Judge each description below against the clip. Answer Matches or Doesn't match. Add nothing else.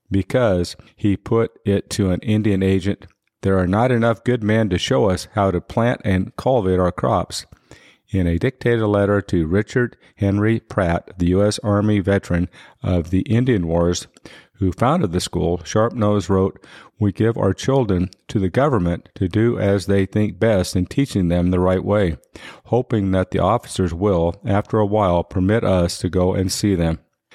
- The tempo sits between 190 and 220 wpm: Doesn't match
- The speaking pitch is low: Matches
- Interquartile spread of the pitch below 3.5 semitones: Matches